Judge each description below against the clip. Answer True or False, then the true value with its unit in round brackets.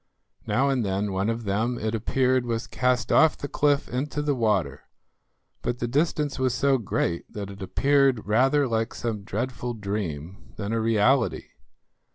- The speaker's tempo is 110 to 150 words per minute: False (165 wpm)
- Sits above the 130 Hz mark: False (115 Hz)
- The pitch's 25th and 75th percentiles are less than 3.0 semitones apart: False (4.3 semitones)